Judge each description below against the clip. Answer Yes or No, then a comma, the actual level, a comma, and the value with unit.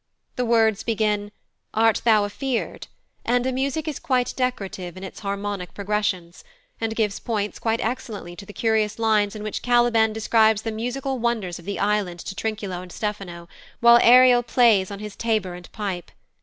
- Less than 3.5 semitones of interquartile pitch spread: Yes, average, 2.9 semitones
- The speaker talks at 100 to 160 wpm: No, average, 170 wpm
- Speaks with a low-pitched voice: No, high, 215 Hz